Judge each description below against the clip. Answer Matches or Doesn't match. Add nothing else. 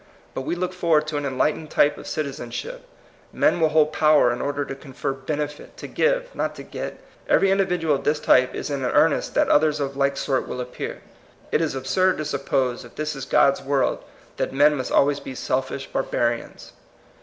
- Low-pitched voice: Doesn't match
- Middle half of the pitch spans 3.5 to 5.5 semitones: Doesn't match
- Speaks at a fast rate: Matches